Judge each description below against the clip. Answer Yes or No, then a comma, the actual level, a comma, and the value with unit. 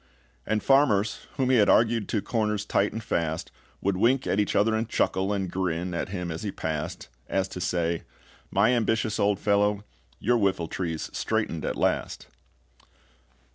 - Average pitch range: Yes, average, 3.5 semitones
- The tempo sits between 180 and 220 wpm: No, average, 165 wpm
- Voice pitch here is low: Yes, low, 100 Hz